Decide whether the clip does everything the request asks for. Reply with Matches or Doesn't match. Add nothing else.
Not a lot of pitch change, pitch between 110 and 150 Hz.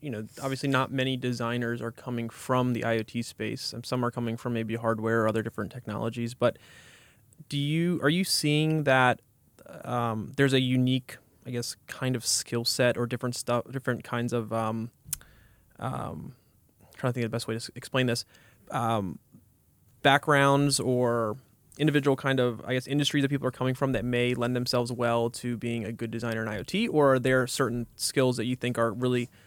Matches